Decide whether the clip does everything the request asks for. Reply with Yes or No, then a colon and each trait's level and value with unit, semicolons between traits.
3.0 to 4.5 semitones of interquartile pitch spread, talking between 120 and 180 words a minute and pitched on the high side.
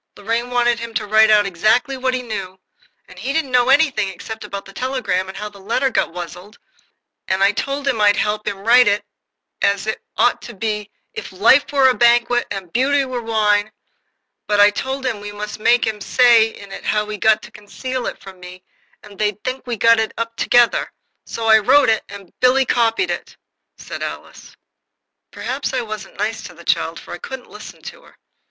No: average, 3.4 semitones; fast, 205 wpm; high, 220 Hz